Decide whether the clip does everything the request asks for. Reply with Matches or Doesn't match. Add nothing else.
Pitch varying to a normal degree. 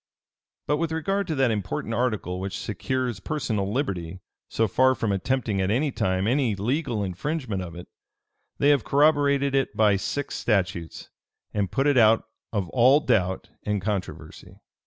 Doesn't match